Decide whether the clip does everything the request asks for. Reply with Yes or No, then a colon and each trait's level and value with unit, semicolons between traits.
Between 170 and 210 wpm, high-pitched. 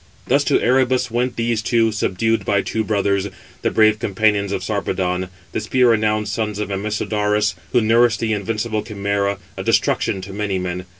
No: average, 175 wpm; low, 105 Hz